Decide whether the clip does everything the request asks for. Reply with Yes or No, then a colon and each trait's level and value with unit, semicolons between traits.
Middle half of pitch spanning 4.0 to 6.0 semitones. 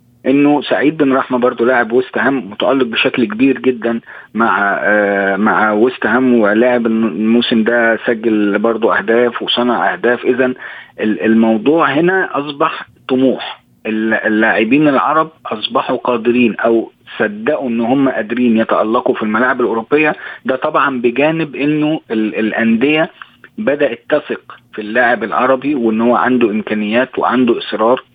No: average, 2.7 semitones